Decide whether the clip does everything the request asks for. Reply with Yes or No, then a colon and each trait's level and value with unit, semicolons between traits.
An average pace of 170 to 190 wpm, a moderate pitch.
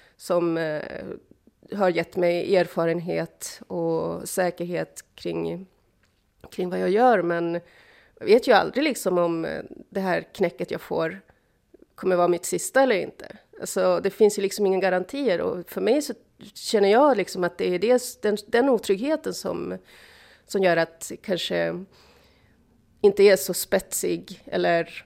No: average, 145 wpm; medium, 180 Hz